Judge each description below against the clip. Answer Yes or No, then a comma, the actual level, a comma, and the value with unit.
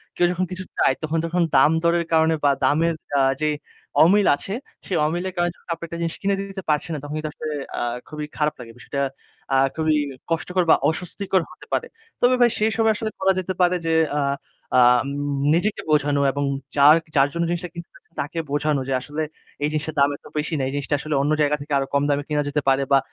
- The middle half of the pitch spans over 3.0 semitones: Yes, average, 3.4 semitones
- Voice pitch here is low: No, medium, 155 Hz